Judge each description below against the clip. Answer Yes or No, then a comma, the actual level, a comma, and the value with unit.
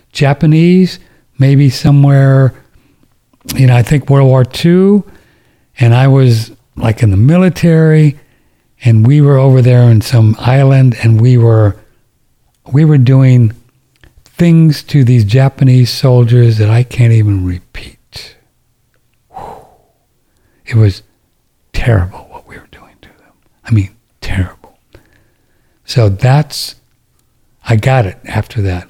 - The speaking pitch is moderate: No, low, 125 Hz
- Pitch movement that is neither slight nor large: Yes, average, 3.4 semitones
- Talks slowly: Yes, slow, 125 wpm